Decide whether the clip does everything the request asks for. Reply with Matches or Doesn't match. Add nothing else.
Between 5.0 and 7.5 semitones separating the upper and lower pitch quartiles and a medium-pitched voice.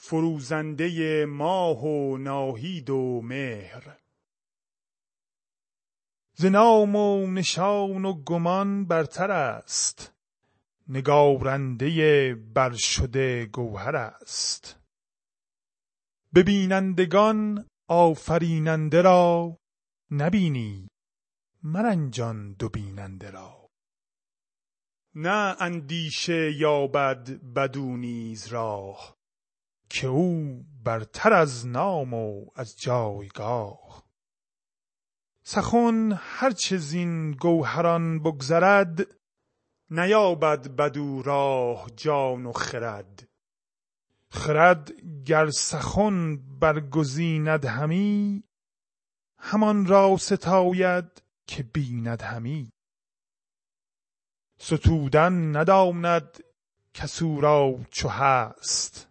Matches